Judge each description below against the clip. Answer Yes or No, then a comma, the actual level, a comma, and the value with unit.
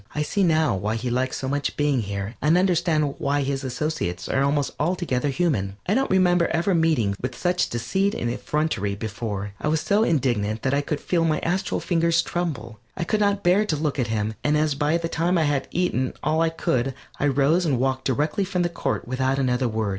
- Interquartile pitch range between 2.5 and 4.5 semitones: No, average, 5.2 semitones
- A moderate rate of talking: No, fast, 215 wpm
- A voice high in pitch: No, medium, 145 Hz